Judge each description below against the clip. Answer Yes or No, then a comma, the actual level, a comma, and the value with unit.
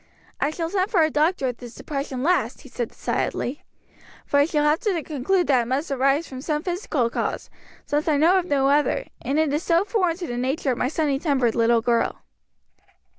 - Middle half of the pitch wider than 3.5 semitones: Yes, average, 4.2 semitones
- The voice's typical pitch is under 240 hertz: No, very high, 295 Hz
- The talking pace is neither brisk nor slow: No, fast, 215 wpm